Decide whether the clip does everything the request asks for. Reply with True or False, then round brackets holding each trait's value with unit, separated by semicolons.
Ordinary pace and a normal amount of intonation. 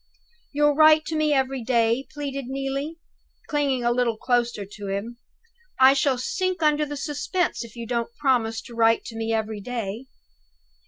True (165 wpm; 4.2 semitones)